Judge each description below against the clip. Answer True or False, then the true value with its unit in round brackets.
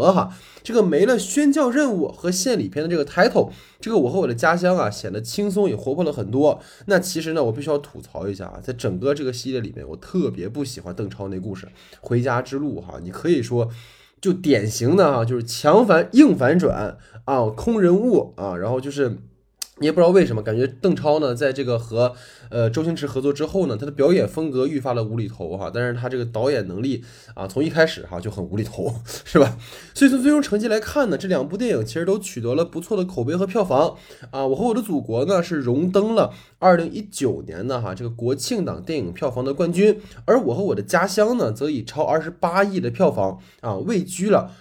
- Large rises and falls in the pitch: True (7.8 semitones)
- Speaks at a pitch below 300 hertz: True (140 Hz)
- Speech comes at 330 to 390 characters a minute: True (335 characters per minute)